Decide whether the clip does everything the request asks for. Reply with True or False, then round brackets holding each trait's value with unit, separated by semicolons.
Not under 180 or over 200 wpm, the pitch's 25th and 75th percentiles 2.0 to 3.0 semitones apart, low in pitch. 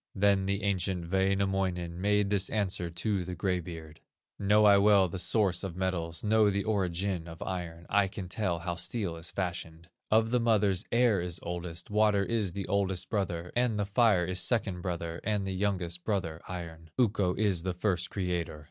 True (185 wpm; 2.7 semitones; 95 Hz)